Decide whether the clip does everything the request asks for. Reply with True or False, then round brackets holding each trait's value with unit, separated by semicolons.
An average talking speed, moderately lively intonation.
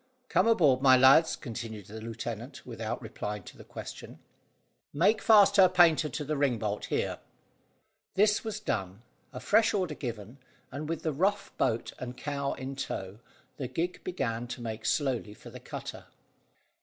False (165 wpm; 6.7 semitones)